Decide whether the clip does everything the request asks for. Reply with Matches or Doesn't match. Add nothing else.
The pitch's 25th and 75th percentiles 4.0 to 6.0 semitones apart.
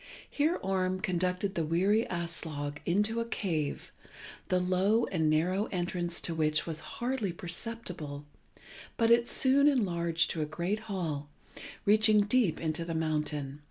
Matches